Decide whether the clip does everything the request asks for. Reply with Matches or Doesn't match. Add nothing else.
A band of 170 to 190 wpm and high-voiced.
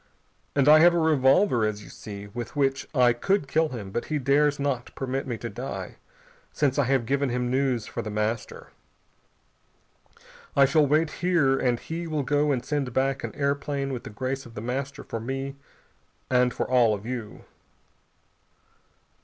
Doesn't match